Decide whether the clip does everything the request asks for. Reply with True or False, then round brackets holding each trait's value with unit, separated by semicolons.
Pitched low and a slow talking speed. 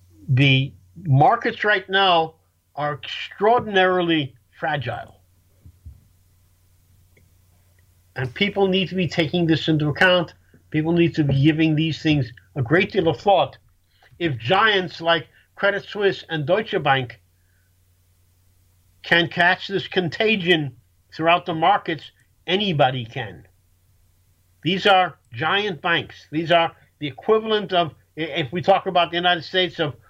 False (155 Hz; 125 wpm)